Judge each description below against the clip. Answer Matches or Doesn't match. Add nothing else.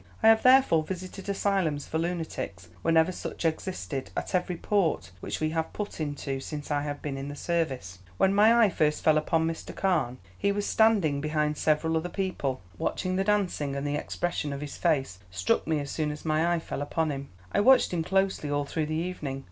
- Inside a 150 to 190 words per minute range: Doesn't match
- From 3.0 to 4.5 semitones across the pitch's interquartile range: Matches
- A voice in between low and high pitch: Matches